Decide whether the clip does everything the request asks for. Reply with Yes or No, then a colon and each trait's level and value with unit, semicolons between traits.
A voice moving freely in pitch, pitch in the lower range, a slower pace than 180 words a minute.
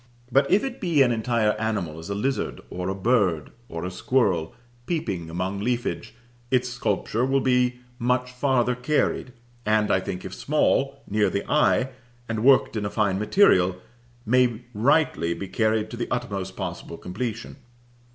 No: average, 4.7 semitones; low, 115 Hz; average, 160 wpm